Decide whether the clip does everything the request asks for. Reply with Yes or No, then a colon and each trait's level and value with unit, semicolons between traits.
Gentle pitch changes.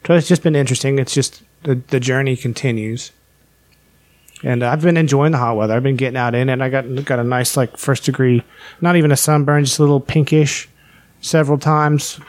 No: average, 3.0 semitones